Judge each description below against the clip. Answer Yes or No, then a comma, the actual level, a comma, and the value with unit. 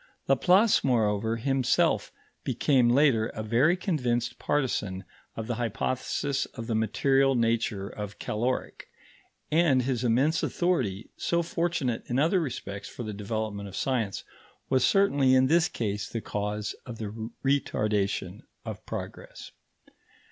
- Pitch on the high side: No, low, 120 Hz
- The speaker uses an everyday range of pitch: Yes, average, 4.4 semitones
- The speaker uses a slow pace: Yes, slow, 130 wpm